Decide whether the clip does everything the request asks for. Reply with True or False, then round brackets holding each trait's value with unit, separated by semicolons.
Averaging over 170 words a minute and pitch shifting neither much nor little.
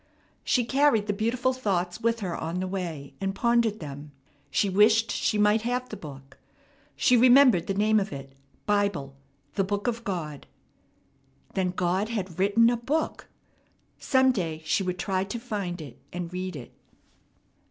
False (165 wpm; 4.7 semitones)